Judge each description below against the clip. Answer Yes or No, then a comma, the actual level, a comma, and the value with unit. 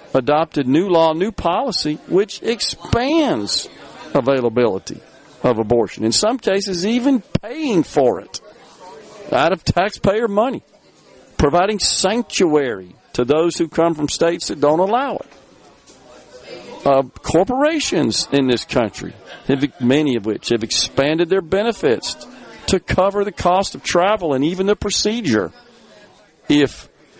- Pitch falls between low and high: Yes, medium, 170 Hz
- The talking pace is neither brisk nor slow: No, slow, 125 wpm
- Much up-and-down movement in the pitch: Yes, wide, 7.0 semitones